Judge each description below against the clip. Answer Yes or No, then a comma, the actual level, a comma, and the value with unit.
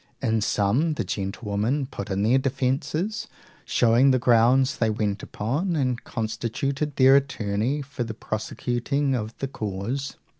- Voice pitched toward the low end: Yes, low, 125 Hz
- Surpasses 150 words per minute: No, average, 140 wpm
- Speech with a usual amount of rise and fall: Yes, average, 4.1 semitones